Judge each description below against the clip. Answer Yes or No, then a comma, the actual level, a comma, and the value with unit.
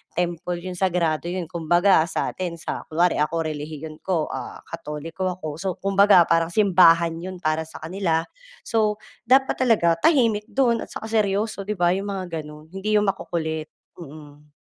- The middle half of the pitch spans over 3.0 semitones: Yes, average, 3.6 semitones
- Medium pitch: Yes, medium, 175 Hz